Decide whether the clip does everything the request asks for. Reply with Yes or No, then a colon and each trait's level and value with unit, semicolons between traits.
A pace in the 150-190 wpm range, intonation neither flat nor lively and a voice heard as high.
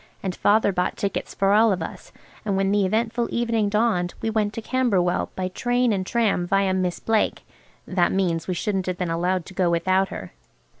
No: average, 200 wpm; average, 3.3 semitones; high, 195 Hz